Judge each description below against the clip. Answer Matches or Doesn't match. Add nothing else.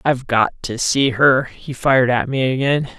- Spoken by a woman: Doesn't match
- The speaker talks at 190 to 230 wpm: Matches